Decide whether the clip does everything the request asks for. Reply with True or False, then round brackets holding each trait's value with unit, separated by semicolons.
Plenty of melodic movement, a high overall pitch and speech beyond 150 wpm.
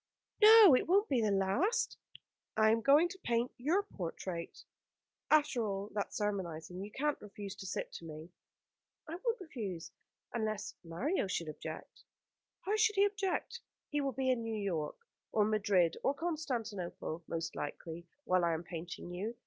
True (8.9 semitones; 215 Hz; 160 wpm)